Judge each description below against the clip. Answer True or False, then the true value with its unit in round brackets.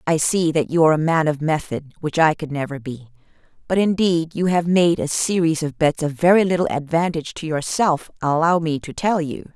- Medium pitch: True (160 Hz)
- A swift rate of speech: True (215 wpm)